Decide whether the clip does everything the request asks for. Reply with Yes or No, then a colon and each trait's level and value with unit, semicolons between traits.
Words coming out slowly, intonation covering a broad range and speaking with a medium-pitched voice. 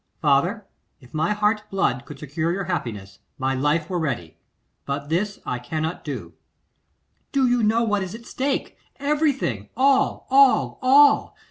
No: average, 150 wpm; wide, 8.8 semitones; medium, 180 Hz